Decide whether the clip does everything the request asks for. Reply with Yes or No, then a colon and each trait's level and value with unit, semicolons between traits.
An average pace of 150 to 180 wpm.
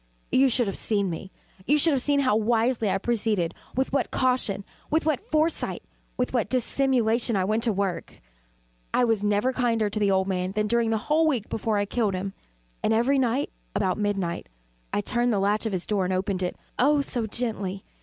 No: fast, 205 wpm